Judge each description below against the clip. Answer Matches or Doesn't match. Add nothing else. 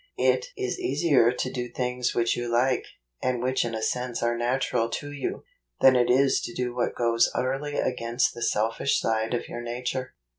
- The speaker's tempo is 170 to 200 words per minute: Matches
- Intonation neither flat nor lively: Doesn't match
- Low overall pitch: Matches